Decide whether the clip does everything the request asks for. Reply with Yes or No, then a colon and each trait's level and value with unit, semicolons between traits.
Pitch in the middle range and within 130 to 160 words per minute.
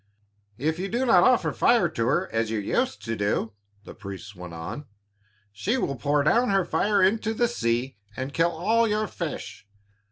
No: medium, 160 Hz; average, 185 wpm